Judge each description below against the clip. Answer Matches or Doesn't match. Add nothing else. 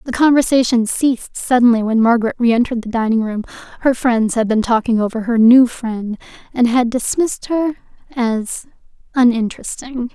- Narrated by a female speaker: Matches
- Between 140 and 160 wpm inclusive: Matches